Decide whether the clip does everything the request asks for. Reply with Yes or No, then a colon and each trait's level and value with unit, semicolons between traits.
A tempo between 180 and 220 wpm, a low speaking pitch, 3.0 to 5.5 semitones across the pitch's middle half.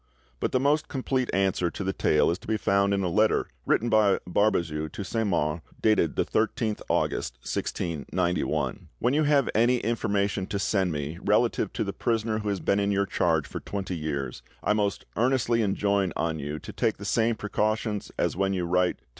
Yes: average, 200 wpm; low, 100 Hz; average, 3.9 semitones